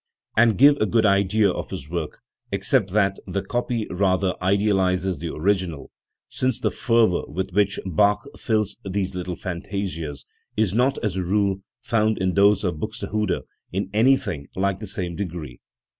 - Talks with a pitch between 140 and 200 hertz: No, low, 100 Hz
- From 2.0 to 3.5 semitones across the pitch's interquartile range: Yes, average, 2.8 semitones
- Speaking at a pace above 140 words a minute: Yes, average, 160 wpm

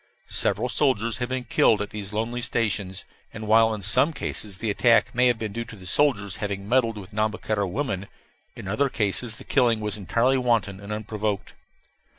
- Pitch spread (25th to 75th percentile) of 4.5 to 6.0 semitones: No, average, 2.9 semitones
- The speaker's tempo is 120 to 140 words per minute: No, average, 190 wpm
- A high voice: No, low, 110 Hz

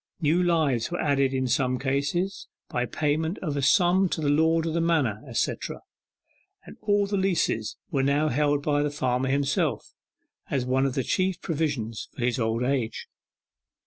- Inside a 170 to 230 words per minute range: Yes, average, 175 wpm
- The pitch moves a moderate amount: Yes, average, 4.0 semitones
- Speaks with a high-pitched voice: No, medium, 145 Hz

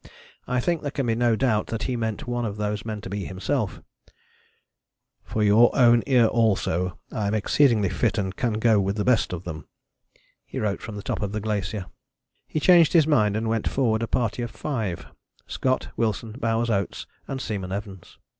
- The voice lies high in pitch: No, low, 110 Hz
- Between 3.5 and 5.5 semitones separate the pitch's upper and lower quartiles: No, average, 2.9 semitones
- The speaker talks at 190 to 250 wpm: Yes, average, 195 wpm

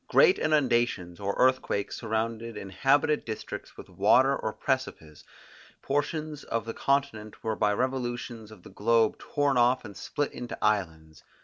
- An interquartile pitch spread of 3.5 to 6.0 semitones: Yes, average, 4.4 semitones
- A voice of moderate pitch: No, low, 115 Hz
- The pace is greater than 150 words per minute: No, average, 140 wpm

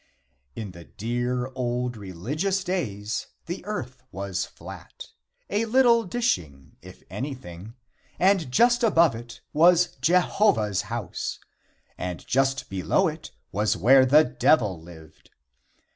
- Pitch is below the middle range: Yes, low, 125 Hz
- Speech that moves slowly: Yes, slow, 120 wpm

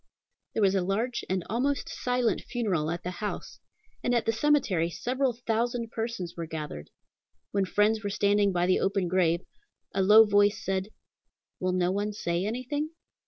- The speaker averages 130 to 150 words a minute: No, average, 165 wpm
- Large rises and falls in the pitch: No, average, 4.1 semitones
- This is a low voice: No, high, 205 Hz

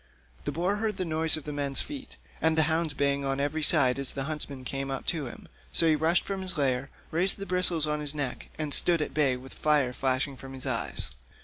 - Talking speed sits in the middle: No, fast, 235 wpm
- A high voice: No, medium, 150 Hz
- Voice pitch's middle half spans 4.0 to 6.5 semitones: No, average, 3.2 semitones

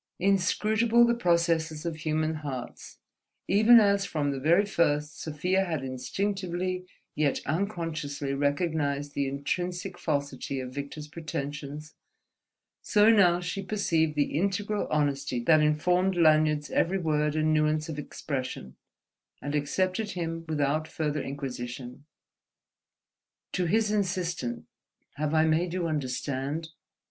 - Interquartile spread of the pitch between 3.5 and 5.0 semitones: Yes, average, 4.1 semitones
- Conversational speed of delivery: No, slow, 120 wpm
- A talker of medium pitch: Yes, medium, 155 Hz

